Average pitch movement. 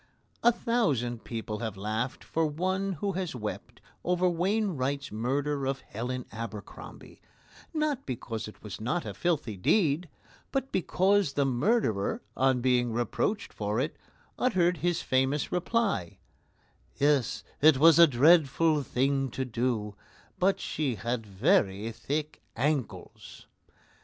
No: wide, 6.9 semitones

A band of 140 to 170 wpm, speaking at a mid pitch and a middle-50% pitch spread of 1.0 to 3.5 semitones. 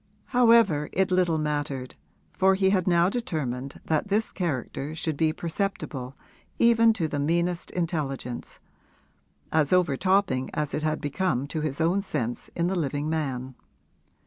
No: average, 145 wpm; medium, 160 Hz; average, 4.5 semitones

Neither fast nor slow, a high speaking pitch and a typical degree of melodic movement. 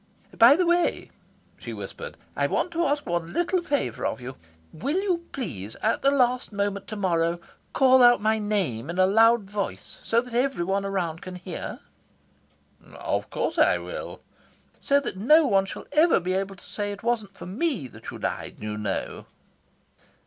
No: average, 180 wpm; high, 210 Hz; wide, 6.8 semitones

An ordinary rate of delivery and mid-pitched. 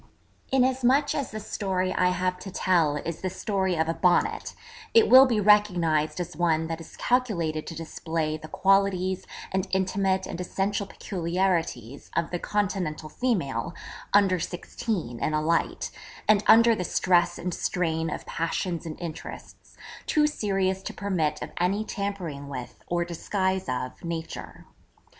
Yes: average, 150 wpm; medium, 180 Hz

